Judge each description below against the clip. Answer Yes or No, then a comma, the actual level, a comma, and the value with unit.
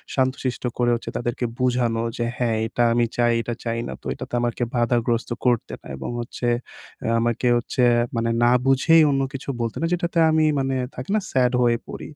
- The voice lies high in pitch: No, low, 120 Hz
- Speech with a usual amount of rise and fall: No, narrow, 1.6 semitones